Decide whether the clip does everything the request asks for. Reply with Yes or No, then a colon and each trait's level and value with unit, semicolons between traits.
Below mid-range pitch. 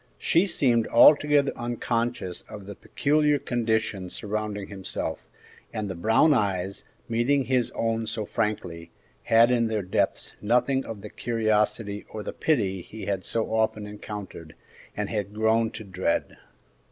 Yes: low, 110 Hz